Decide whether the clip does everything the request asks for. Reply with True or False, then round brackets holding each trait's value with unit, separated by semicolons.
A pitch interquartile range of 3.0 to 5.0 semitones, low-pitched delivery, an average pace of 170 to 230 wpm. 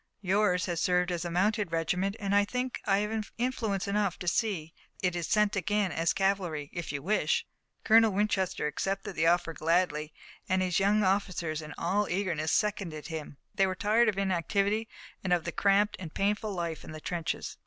False (3.4 semitones; 190 Hz; 190 wpm)